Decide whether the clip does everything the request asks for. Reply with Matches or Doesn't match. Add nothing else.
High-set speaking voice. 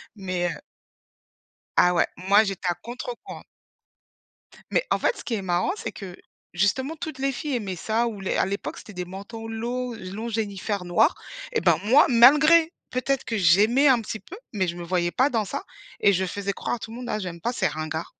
Matches